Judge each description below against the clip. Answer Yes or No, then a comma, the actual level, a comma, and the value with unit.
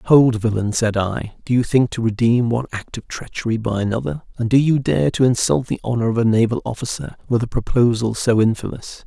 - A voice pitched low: Yes, low, 115 Hz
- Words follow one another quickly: Yes, fast, 210 wpm